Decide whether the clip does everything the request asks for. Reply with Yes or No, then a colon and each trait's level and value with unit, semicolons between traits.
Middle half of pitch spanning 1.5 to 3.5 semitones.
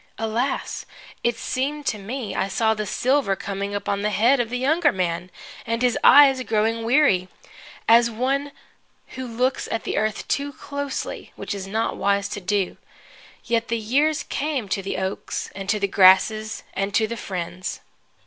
No: average, 4.4 semitones